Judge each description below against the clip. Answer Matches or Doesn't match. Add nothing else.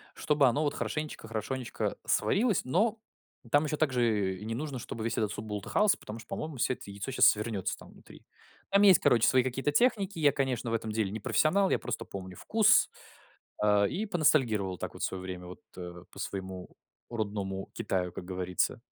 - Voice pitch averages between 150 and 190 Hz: Doesn't match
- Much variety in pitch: Matches